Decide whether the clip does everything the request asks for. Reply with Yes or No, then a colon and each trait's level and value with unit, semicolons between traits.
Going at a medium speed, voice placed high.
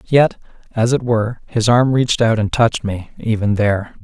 No: average, 195 wpm; low, 115 Hz